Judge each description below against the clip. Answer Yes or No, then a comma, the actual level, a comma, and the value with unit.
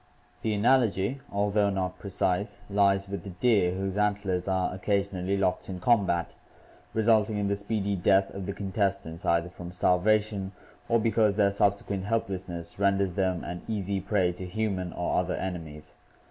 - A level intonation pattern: Yes, narrow, 2.0 semitones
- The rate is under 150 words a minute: No, average, 160 wpm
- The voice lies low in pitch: Yes, low, 100 Hz